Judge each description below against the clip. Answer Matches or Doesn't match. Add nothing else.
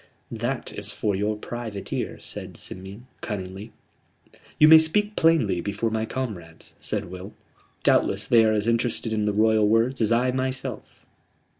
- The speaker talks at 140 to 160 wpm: Matches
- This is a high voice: Doesn't match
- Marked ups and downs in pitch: Doesn't match